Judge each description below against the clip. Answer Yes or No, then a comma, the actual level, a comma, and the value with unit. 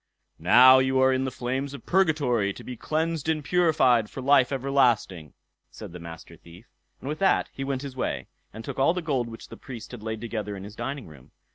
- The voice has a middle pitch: No, low, 130 Hz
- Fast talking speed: Yes, fast, 220 wpm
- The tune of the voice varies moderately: Yes, average, 4.0 semitones